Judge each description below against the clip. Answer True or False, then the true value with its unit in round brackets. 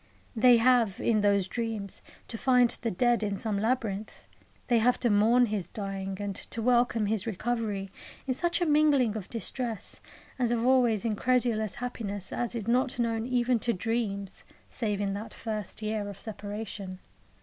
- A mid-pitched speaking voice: False (225 Hz)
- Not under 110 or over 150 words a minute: False (165 wpm)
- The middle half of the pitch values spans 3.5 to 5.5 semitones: False (3.0 semitones)